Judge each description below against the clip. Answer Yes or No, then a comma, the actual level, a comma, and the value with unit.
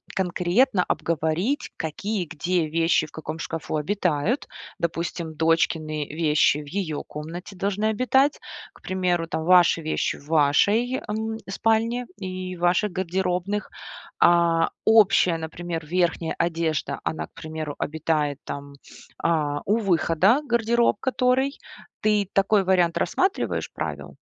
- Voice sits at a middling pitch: Yes, medium, 175 Hz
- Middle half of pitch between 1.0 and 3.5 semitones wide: No, average, 4.3 semitones